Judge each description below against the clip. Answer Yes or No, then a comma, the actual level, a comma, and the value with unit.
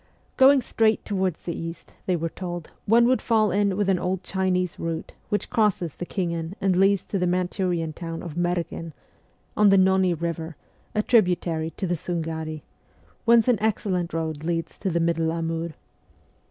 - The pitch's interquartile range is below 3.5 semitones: Yes, average, 2.9 semitones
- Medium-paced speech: Yes, average, 170 wpm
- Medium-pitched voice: Yes, medium, 180 Hz